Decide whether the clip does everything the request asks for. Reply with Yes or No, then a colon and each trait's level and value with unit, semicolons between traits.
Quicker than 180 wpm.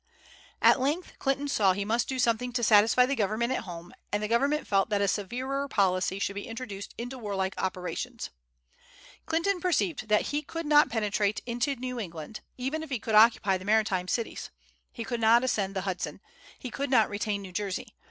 Yes: average, 190 wpm